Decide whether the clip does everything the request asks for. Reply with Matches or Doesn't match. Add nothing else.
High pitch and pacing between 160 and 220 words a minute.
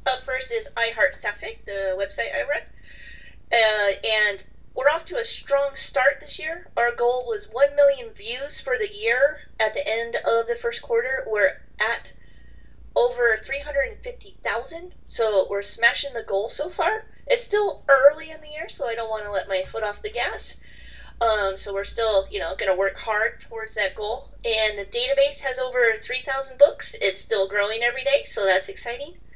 Matches